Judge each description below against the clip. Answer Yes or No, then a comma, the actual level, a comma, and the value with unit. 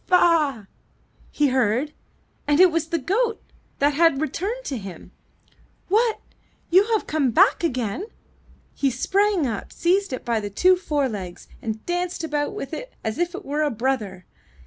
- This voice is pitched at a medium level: No, very high, 300 Hz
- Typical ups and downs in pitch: No, wide, 6.4 semitones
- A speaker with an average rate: Yes, average, 170 wpm